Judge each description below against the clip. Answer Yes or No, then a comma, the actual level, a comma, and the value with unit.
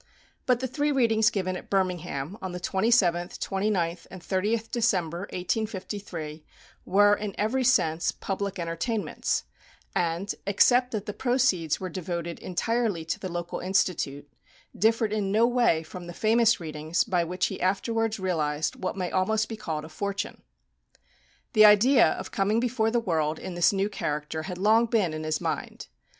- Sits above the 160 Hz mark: Yes, high, 190 Hz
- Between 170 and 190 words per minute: No, average, 160 wpm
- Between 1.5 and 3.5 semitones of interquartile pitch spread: No, average, 4.3 semitones